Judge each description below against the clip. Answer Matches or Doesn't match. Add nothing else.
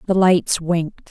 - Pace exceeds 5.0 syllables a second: Doesn't match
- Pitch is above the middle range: Doesn't match